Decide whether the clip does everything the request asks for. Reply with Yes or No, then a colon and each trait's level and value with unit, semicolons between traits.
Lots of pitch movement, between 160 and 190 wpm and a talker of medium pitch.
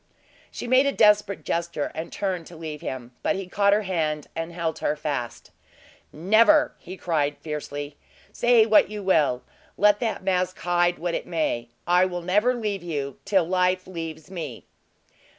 No: average, 4.2 semitones; average, 170 wpm; medium, 175 Hz